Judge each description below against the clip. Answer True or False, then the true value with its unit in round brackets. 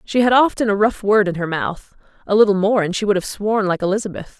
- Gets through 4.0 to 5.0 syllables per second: False (6.0 syllables/s)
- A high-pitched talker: True (205 Hz)